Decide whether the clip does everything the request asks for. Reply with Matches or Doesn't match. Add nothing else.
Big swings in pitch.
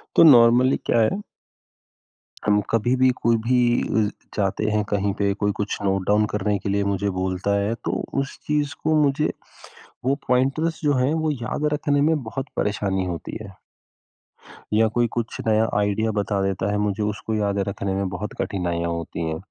Doesn't match